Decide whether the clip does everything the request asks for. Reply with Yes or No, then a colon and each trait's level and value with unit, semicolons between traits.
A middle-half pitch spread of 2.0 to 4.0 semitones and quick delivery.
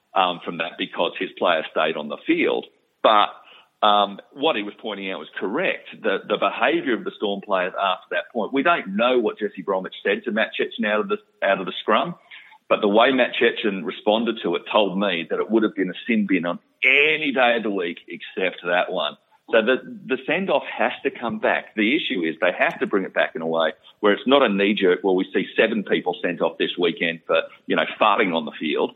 Yes: average, 3.4 semitones; fast, 240 wpm